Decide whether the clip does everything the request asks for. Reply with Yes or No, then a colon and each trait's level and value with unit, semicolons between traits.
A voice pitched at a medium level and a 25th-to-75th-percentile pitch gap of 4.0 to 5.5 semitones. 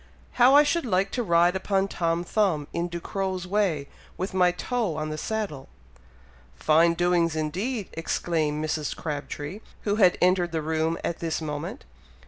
No: medium, 175 Hz; average, 3.6 semitones